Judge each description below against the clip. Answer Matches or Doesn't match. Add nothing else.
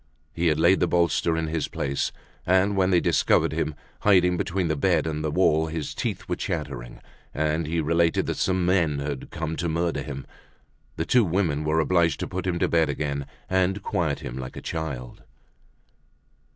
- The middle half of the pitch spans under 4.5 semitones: Matches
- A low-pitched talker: Matches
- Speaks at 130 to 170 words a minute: Doesn't match